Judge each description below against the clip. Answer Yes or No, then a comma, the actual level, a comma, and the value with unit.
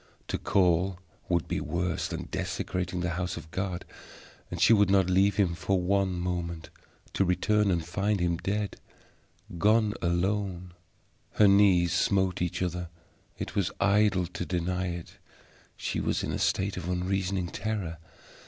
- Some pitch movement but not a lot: No, narrow, 2.2 semitones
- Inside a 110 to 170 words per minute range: Yes, average, 155 wpm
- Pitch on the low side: Yes, very low, 90 Hz